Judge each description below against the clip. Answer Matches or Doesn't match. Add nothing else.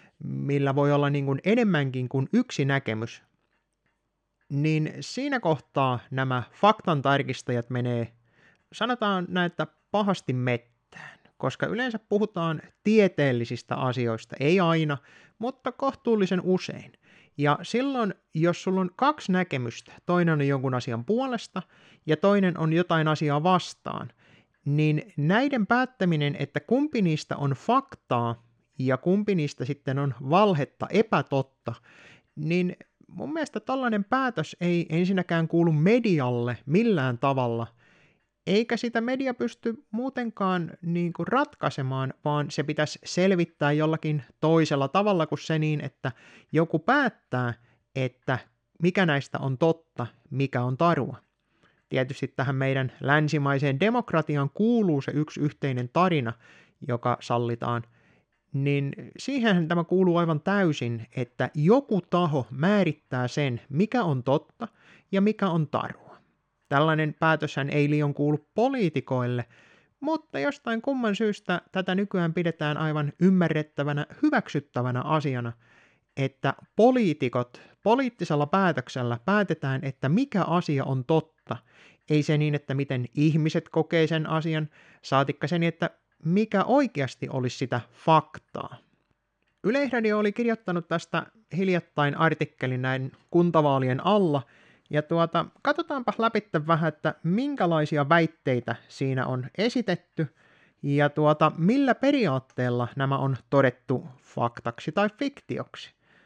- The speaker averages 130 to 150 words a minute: Doesn't match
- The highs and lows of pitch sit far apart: Matches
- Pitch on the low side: Doesn't match